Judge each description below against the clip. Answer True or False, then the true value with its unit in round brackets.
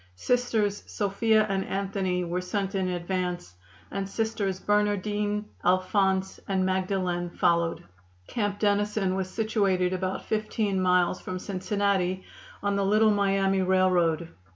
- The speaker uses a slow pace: True (120 wpm)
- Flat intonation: True (1.9 semitones)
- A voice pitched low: False (195 Hz)